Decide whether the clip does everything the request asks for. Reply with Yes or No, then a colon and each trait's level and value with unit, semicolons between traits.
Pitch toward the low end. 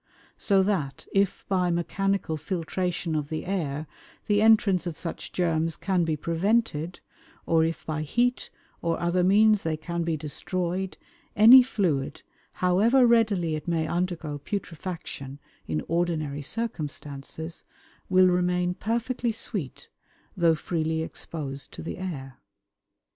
No: medium, 175 Hz